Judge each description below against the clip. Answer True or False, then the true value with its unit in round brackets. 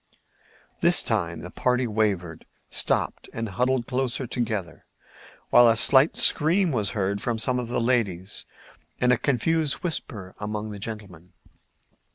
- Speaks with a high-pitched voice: False (115 Hz)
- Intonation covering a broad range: False (3.8 semitones)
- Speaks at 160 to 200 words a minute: False (140 wpm)